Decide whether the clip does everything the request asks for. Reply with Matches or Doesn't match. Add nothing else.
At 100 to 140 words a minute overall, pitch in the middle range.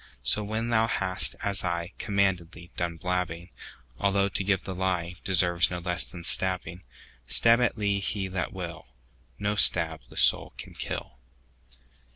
Doesn't match